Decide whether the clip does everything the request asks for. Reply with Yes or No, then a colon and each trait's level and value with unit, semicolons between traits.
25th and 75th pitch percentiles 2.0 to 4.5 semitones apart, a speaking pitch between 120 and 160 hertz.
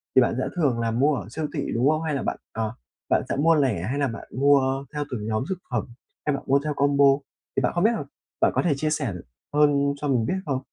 Yes: average, 3.2 semitones; medium, 140 Hz